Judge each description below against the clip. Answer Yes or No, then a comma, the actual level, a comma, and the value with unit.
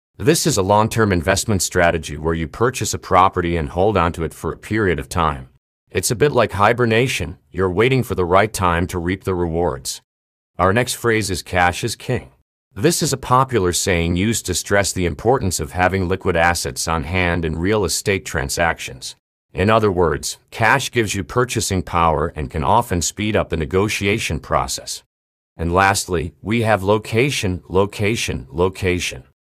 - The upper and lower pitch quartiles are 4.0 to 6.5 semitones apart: Yes, average, 4.4 semitones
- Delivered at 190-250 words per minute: No, average, 175 wpm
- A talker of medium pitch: No, very low, 90 Hz